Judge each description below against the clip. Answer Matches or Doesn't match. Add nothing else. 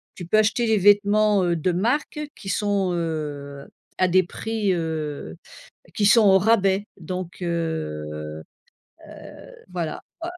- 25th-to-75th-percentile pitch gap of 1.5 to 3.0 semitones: Doesn't match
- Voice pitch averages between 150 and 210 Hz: Matches